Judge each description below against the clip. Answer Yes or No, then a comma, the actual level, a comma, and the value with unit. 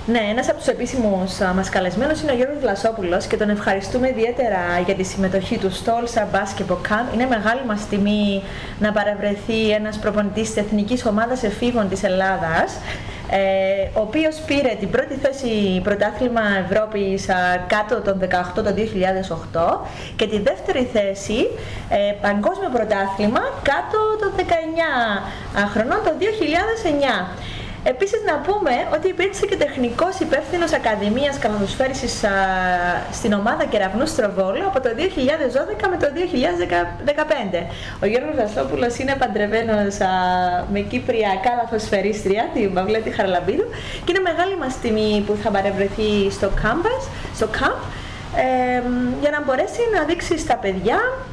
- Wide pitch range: Yes, wide, 5.9 semitones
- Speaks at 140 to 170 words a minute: No, average, 130 wpm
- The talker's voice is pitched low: No, high, 220 Hz